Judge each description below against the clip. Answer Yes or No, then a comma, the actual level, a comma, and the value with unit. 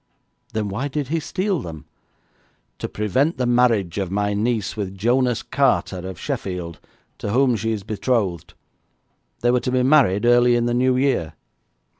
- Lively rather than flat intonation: No, average, 4.5 semitones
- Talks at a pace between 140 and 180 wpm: Yes, average, 165 wpm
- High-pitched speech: No, low, 115 Hz